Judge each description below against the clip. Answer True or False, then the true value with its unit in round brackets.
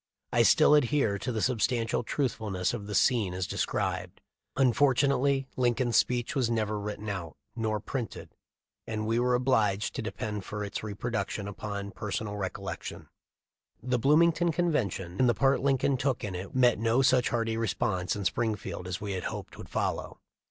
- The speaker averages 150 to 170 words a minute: True (165 wpm)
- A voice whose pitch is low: True (115 Hz)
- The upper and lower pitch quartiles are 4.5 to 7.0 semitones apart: False (3.9 semitones)